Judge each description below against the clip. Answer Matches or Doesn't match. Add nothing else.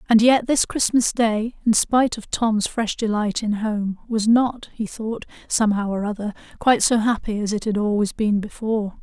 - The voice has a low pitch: Doesn't match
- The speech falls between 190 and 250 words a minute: Matches